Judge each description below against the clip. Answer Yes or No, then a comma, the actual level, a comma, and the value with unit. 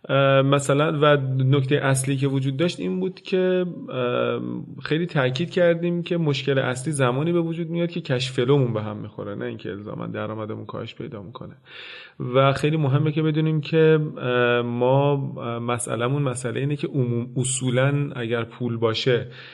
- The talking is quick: No, average, 145 wpm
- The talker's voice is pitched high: No, low, 135 Hz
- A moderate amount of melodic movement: Yes, average, 3.9 semitones